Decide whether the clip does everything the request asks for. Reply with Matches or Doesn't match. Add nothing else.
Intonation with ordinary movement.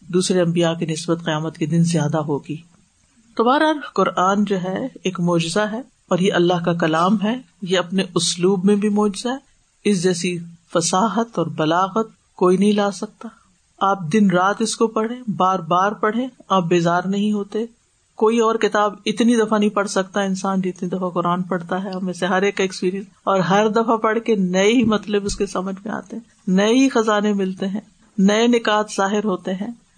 Matches